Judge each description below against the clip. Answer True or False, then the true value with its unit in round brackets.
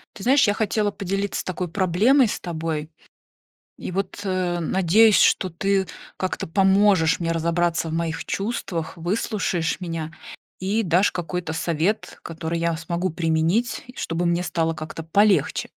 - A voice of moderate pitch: True (175 Hz)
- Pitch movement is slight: False (3.3 semitones)